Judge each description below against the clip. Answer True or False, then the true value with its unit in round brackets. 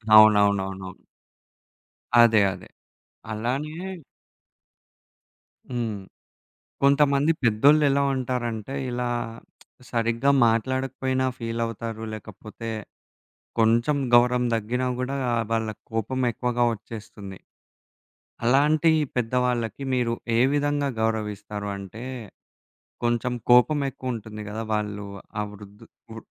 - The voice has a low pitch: True (115 Hz)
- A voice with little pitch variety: False (3.3 semitones)